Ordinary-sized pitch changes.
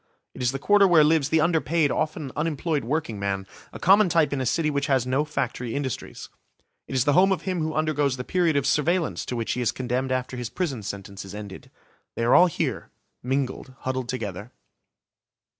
Yes: average, 4.3 semitones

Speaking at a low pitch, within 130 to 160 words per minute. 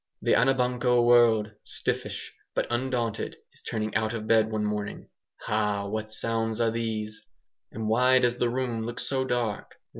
Yes: low, 115 Hz; average, 155 wpm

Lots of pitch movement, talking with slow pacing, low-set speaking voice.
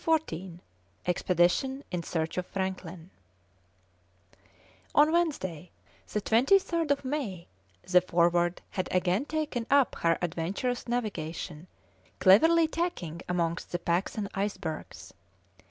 No: wide, 7.8 semitones; slow, 110 wpm; high, 190 Hz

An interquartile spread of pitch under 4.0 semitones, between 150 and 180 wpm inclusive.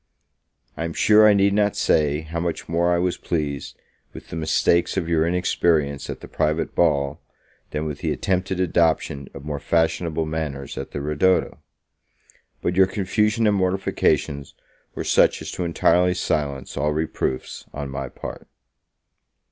Yes: average, 3.4 semitones; average, 155 wpm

